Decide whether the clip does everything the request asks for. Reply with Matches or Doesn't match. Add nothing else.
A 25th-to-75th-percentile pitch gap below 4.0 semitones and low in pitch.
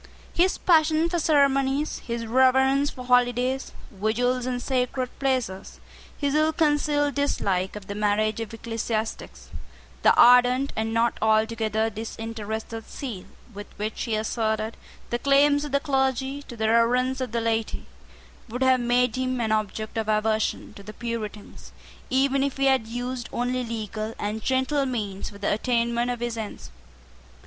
Doesn't match